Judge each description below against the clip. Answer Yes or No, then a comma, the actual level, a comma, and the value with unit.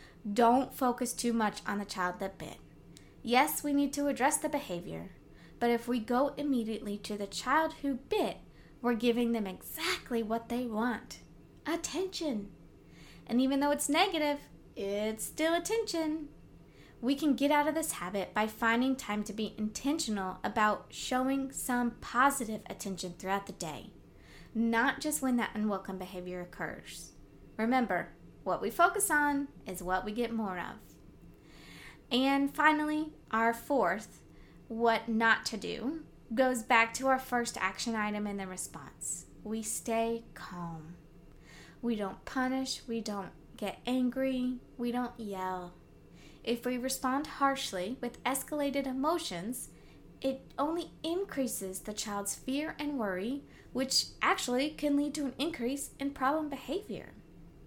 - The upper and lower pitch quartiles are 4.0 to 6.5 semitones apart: Yes, average, 4.9 semitones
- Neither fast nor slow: Yes, average, 145 wpm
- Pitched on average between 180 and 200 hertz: No, high, 245 Hz